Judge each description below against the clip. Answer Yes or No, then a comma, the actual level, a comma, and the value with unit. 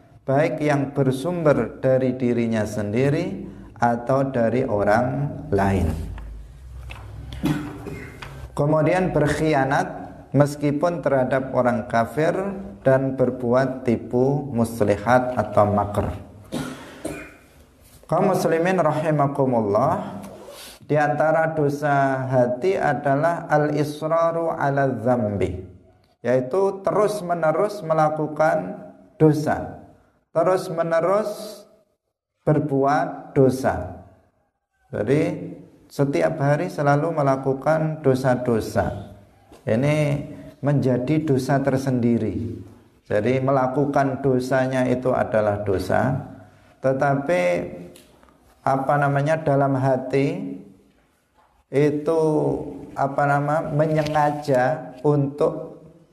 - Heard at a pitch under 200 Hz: Yes, low, 135 Hz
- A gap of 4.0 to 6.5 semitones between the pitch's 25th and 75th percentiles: Yes, average, 4.3 semitones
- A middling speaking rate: No, slow, 70 wpm